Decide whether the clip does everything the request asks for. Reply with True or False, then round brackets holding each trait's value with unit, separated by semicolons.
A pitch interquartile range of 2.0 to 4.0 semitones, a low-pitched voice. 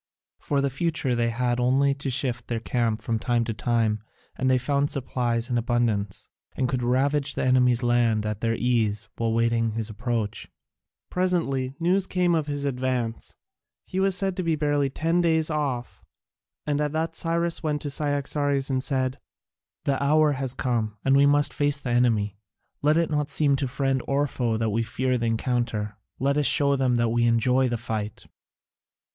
True (3.6 semitones; 130 Hz)